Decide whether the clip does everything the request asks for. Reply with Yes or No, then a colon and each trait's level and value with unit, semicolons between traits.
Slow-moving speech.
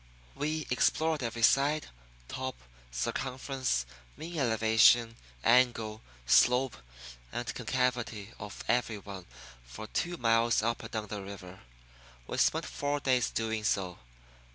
Yes: slow, 120 wpm